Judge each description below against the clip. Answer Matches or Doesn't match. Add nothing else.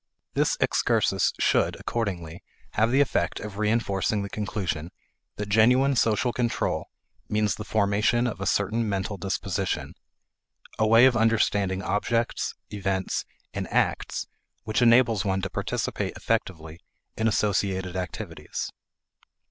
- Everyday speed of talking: Doesn't match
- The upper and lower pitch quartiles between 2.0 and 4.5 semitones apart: Matches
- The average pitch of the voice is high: Doesn't match